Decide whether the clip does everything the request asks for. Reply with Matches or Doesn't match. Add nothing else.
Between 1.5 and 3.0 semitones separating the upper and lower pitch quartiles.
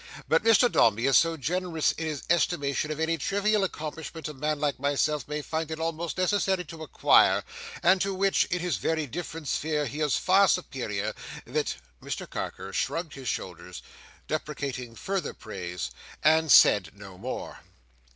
Doesn't match